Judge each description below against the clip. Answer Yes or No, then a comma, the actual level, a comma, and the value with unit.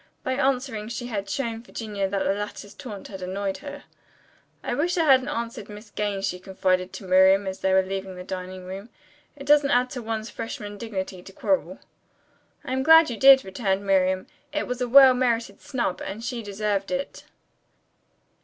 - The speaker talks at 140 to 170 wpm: No, average, 185 wpm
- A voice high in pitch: Yes, high, 210 Hz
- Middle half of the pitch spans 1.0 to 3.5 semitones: No, average, 4.8 semitones